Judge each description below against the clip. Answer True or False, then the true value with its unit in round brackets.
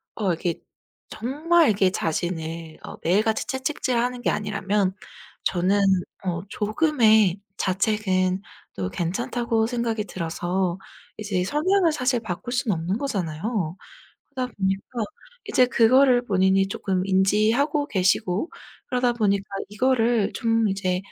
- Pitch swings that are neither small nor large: True (4.7 semitones)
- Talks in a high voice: True (210 Hz)